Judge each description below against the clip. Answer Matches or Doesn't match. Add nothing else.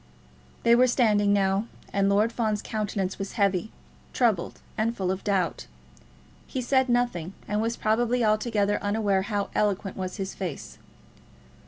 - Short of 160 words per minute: Matches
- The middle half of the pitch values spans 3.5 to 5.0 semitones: Doesn't match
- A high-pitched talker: Matches